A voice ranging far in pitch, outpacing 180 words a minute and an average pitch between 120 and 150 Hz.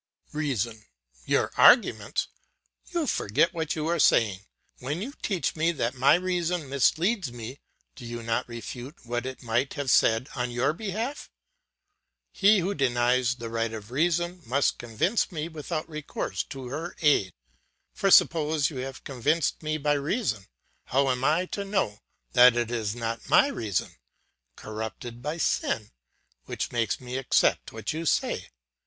No: wide, 5.8 semitones; average, 155 wpm; low, 135 Hz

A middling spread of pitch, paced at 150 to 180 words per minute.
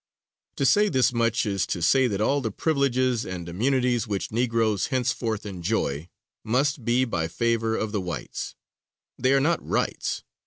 Yes: average, 3.9 semitones; average, 160 wpm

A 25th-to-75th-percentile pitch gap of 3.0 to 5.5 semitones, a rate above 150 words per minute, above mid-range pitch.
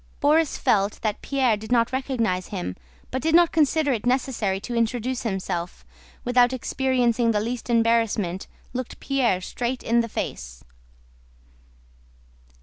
No: average, 3.6 semitones; average, 140 wpm; high, 235 Hz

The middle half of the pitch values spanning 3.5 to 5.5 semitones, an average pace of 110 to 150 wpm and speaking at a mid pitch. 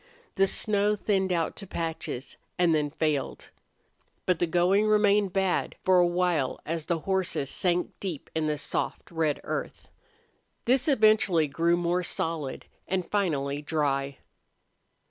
Yes: average, 3.8 semitones; average, 140 wpm; medium, 175 Hz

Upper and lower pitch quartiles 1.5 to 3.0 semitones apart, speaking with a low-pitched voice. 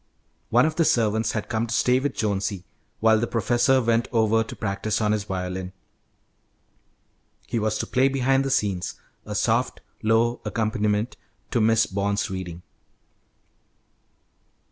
Yes: narrow, 2.6 semitones; low, 110 Hz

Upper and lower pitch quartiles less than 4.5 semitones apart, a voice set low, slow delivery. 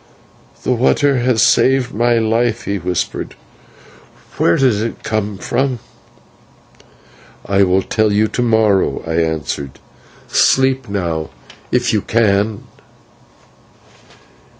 Yes: average, 3.8 semitones; low, 110 Hz; slow, 105 wpm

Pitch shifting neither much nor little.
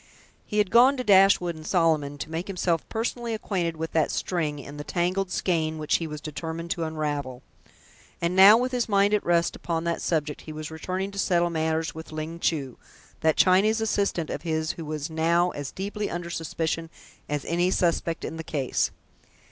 Yes: average, 3.1 semitones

